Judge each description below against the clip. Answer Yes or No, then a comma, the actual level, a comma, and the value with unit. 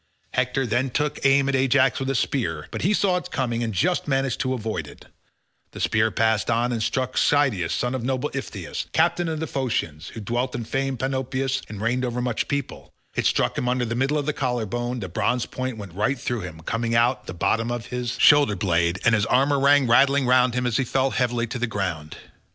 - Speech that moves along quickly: Yes, fast, 225 wpm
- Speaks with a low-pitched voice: Yes, low, 125 Hz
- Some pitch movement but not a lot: Yes, average, 3.1 semitones